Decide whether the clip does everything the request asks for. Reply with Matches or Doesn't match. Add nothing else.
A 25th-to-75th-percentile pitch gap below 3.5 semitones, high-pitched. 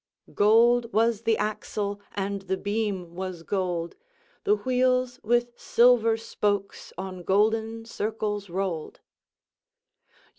Matches